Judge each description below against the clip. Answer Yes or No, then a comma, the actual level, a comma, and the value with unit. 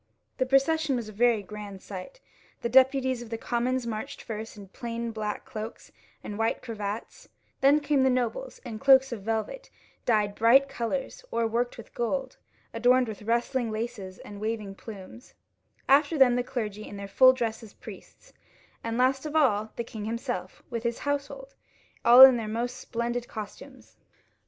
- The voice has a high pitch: Yes, high, 235 Hz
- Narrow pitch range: No, average, 3.2 semitones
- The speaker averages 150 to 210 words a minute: Yes, average, 170 wpm